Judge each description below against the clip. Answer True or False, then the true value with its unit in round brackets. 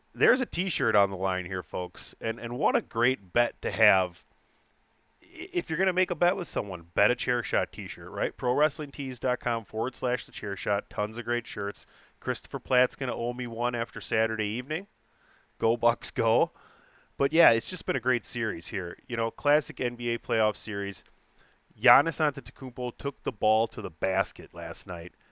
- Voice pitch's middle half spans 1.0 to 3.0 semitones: False (3.7 semitones)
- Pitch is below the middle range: True (120 Hz)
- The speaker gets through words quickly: False (180 wpm)